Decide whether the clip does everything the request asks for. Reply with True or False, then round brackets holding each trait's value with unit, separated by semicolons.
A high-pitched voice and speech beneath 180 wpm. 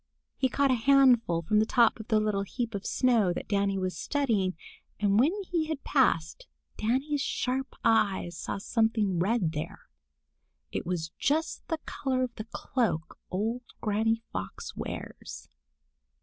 True (225 Hz; 150 wpm)